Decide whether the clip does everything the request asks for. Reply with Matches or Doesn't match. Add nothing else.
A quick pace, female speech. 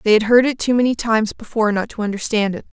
Matches